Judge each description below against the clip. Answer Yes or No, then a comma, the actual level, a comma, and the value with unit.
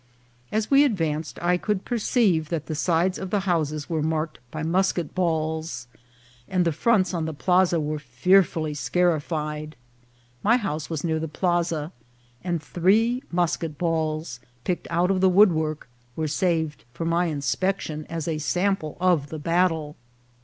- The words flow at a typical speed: Yes, average, 160 wpm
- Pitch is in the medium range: Yes, medium, 165 Hz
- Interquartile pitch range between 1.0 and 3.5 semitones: Yes, average, 3.0 semitones